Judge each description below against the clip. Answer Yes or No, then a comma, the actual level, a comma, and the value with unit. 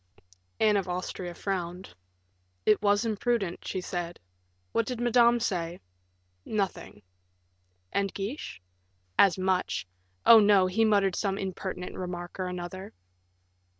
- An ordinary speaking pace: No, slow, 115 wpm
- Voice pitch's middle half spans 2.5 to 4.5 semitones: Yes, average, 2.8 semitones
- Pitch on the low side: No, high, 195 Hz